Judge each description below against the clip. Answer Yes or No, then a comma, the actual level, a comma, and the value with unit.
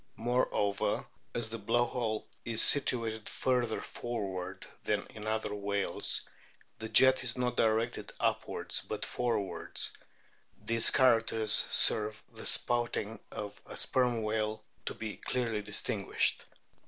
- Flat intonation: Yes, narrow, 2.2 semitones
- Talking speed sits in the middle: No, slow, 120 wpm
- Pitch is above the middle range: No, low, 110 Hz